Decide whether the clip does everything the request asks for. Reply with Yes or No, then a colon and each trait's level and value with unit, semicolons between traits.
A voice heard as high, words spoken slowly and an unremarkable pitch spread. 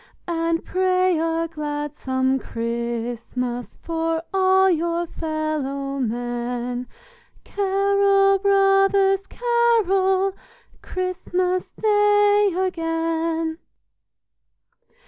Yes: very high, 335 Hz; slow, 65 wpm; average, 5.0 semitones